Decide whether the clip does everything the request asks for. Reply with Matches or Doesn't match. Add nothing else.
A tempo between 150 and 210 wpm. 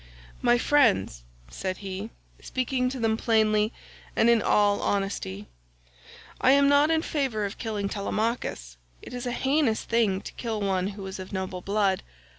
Matches